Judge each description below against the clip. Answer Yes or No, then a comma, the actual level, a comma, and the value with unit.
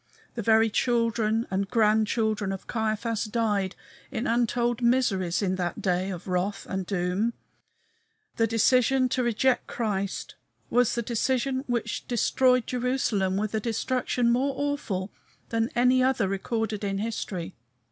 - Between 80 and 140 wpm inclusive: Yes, slow, 135 wpm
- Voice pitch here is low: No, high, 225 Hz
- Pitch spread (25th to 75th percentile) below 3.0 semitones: No, average, 3.6 semitones